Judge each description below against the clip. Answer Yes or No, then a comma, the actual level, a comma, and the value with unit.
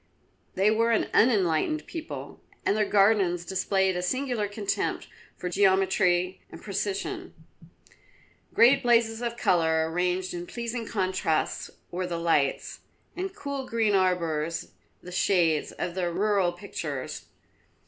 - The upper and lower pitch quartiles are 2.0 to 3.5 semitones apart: No, average, 4.2 semitones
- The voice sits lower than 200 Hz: Yes, high, 190 Hz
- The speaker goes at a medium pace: No, slow, 125 wpm